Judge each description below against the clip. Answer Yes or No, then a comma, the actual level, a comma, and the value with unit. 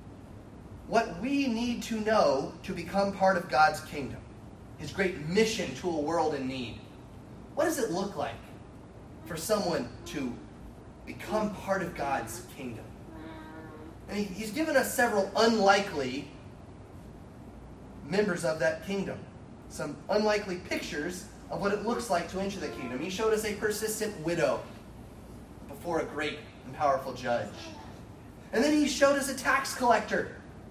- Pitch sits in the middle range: Yes, medium, 175 Hz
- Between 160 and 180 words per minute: No, average, 145 wpm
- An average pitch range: No, wide, 8.7 semitones